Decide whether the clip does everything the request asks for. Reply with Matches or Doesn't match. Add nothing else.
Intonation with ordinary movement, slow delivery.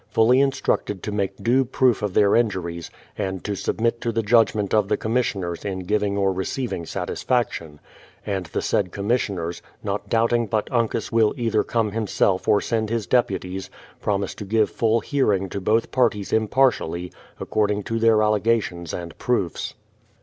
Doesn't match